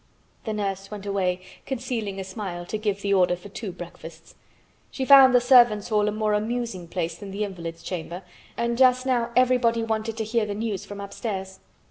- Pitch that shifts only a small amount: No, average, 3.5 semitones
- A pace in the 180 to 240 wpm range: Yes, average, 190 wpm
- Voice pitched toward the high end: Yes, high, 210 Hz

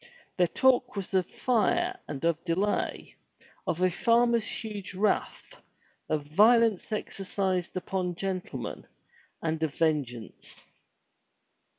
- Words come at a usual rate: No, slow, 105 wpm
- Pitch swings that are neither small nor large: Yes, average, 4.8 semitones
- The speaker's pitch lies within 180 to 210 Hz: Yes, high, 190 Hz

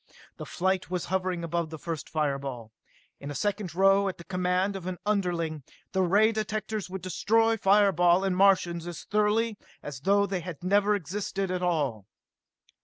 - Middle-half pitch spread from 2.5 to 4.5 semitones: Yes, average, 2.9 semitones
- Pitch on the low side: No, medium, 185 Hz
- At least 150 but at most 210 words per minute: Yes, average, 175 wpm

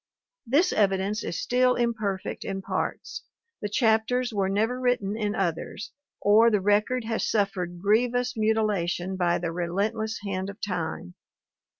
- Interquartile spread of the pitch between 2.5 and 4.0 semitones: Yes, average, 3.0 semitones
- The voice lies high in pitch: Yes, high, 210 Hz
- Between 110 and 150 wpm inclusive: Yes, slow, 135 wpm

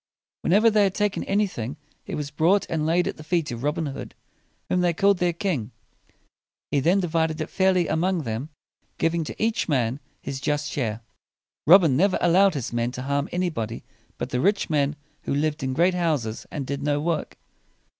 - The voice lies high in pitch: No, medium, 160 Hz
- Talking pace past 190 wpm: Yes, average, 200 wpm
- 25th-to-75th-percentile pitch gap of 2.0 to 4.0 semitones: No, average, 4.4 semitones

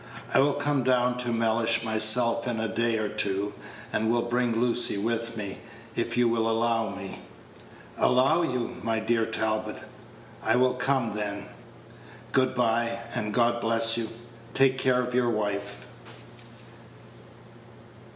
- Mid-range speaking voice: No, low, 115 Hz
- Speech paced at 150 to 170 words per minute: No, average, 140 wpm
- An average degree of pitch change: No, narrow, 1.9 semitones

